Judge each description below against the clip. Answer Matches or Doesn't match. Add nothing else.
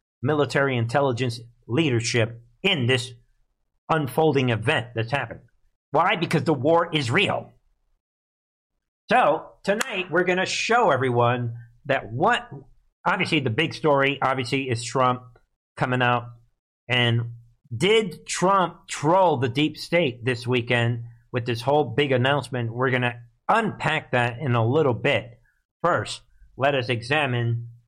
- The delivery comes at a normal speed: Doesn't match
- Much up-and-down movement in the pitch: Doesn't match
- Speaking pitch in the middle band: Doesn't match